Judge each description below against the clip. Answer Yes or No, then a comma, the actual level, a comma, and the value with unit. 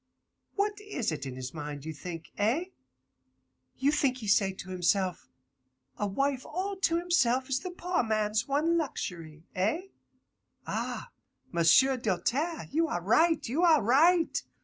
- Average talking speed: Yes, average, 150 wpm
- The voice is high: Yes, very high, 255 Hz